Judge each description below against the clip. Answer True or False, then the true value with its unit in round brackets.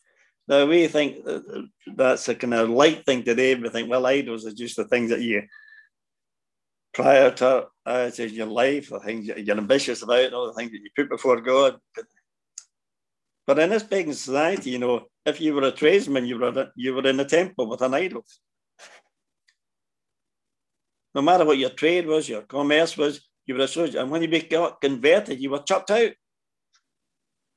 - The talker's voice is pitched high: False (135 Hz)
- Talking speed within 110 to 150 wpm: False (180 wpm)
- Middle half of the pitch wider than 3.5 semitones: True (4.1 semitones)